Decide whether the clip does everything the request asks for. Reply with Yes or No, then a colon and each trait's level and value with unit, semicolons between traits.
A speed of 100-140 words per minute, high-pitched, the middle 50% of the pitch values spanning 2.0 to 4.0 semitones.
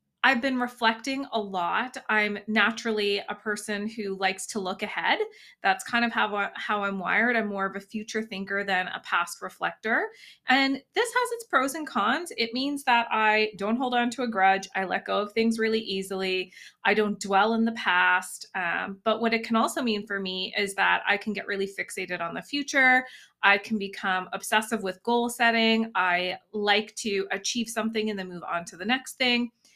No: average, 200 wpm; high, 215 Hz; average, 3.4 semitones